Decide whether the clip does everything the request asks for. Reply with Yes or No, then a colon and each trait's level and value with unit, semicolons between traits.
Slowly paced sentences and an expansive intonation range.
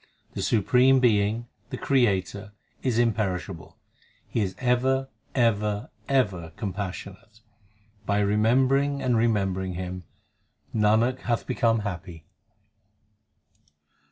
No: slow, 95 wpm; average, 4.1 semitones